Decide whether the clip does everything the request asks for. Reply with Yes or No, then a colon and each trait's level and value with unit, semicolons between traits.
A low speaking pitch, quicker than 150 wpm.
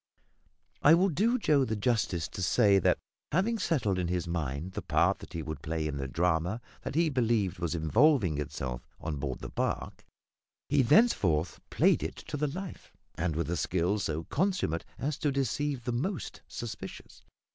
Yes: low, 100 Hz; average, 180 wpm